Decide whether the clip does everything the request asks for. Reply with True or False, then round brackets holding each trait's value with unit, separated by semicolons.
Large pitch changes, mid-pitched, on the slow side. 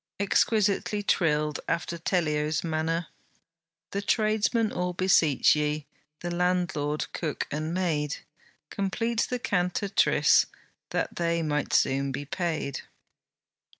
False (4.3 semitones; 170 Hz; 105 wpm)